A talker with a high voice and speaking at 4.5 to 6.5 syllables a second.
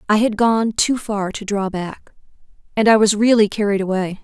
Yes: high, 210 Hz; 5.0 syllables/s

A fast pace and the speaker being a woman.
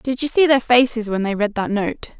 Yes: fast, 275 wpm; female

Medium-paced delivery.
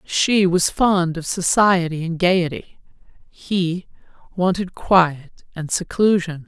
No: slow, 110 wpm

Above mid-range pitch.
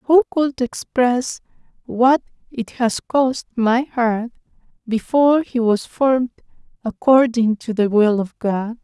Yes: high, 240 Hz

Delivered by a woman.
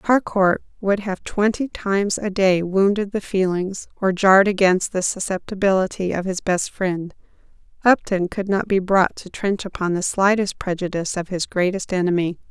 Yes: female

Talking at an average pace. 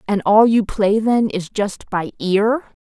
Yes: average, 190 wpm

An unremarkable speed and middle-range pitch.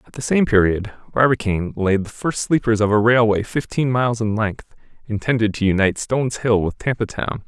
No: average, 195 wpm; low, 110 Hz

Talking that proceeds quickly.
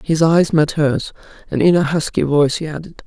Yes: fast, 215 wpm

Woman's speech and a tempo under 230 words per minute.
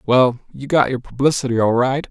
No: male; average, 200 wpm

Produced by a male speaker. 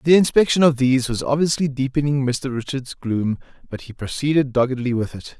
Yes: male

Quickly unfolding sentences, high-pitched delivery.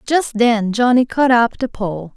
No: average, 195 wpm; high, 235 Hz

